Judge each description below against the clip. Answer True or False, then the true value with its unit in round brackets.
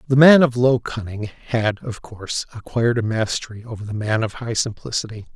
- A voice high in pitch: False (115 Hz)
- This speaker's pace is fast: False (190 wpm)